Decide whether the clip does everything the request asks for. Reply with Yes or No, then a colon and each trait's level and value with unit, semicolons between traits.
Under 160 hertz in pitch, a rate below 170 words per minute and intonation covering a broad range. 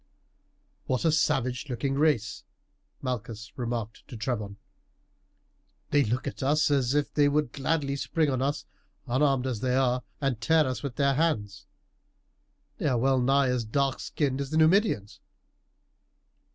No: low, 135 Hz; average, 150 wpm; average, 3.1 semitones